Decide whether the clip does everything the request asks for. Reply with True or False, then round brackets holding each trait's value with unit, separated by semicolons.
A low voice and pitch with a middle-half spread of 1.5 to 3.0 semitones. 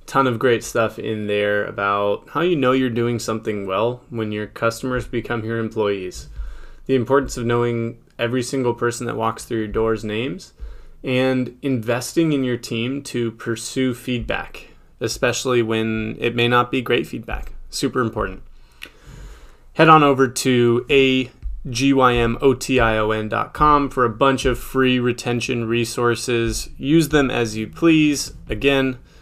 True (120 Hz; 2.5 semitones)